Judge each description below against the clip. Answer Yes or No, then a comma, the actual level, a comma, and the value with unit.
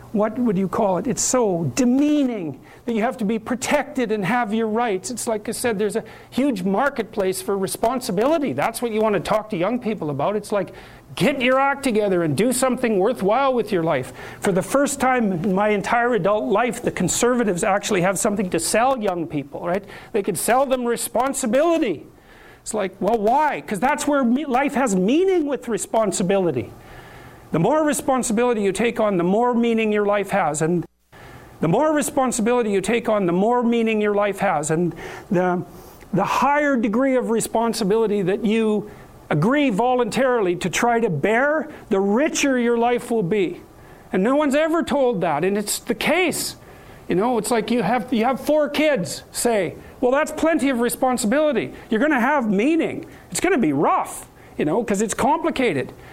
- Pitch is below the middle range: No, high, 230 Hz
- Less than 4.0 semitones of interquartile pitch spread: No, average, 4.5 semitones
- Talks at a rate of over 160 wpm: Yes, average, 185 wpm